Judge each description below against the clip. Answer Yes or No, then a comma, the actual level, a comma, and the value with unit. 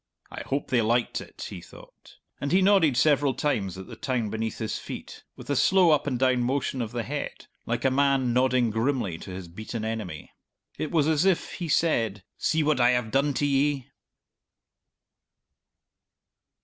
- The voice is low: Yes, low, 130 Hz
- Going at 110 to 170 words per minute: No, average, 180 wpm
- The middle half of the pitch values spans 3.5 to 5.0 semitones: Yes, average, 4.4 semitones